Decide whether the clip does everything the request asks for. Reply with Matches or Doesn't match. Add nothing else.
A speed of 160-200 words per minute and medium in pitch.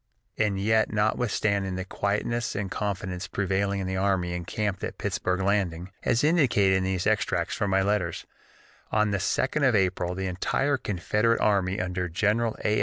Doesn't match